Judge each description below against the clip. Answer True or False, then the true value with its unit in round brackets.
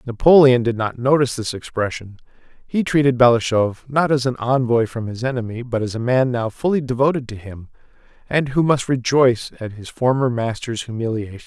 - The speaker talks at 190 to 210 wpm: False (180 wpm)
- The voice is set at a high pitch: False (125 Hz)